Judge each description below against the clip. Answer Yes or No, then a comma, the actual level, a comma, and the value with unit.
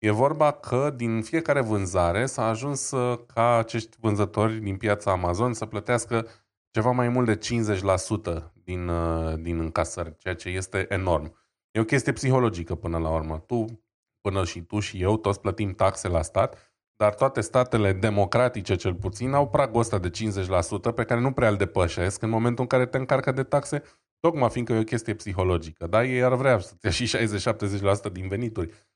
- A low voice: Yes, low, 110 Hz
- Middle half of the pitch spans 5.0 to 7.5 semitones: No, average, 4.1 semitones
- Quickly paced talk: Yes, fast, 180 wpm